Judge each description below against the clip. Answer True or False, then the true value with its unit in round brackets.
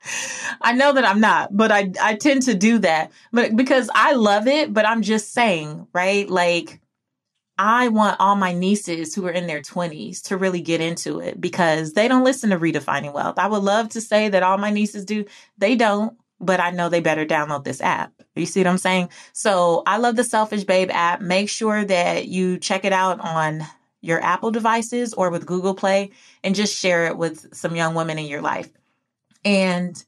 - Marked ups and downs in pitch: False (3.8 semitones)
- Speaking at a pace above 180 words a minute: True (205 wpm)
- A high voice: True (195 Hz)